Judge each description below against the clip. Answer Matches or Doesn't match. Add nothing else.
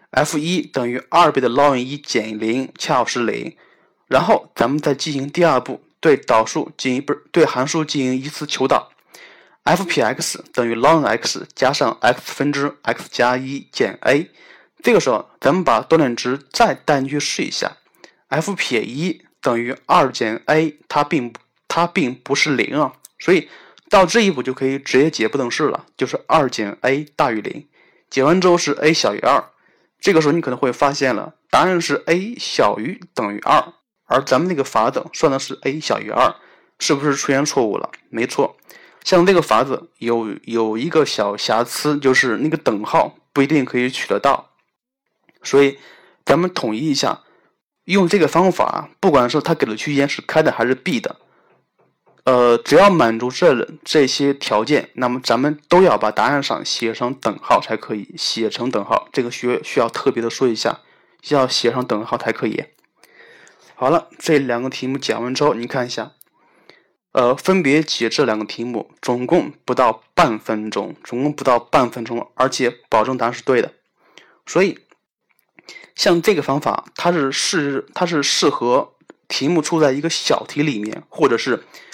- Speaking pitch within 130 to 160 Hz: Matches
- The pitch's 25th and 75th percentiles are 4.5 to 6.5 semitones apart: Doesn't match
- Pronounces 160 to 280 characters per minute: Matches